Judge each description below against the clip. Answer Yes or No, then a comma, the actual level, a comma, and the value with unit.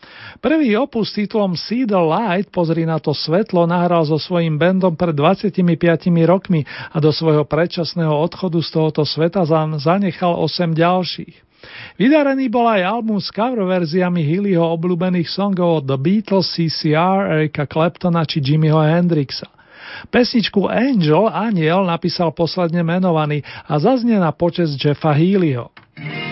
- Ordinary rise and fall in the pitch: Yes, average, 3.2 semitones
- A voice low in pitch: No, medium, 175 Hz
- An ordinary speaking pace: Yes, average, 135 wpm